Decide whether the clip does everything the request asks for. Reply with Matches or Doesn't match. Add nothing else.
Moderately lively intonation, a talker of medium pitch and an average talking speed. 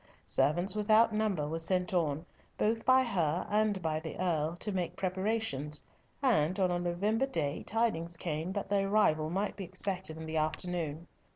Matches